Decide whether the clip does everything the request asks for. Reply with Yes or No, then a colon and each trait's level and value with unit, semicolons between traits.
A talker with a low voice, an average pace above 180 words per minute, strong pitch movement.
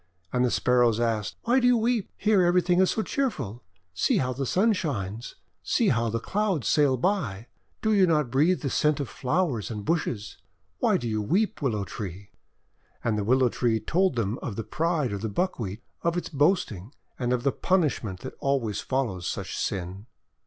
Yes: low, 130 Hz; average, 190 wpm; wide, 8.0 semitones